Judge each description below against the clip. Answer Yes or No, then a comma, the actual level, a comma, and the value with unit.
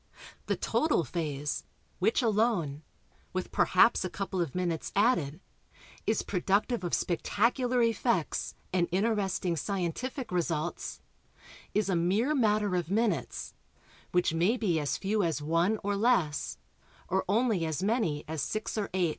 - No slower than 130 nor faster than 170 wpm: Yes, average, 140 wpm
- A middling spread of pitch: Yes, average, 4.6 semitones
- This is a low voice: No, high, 190 Hz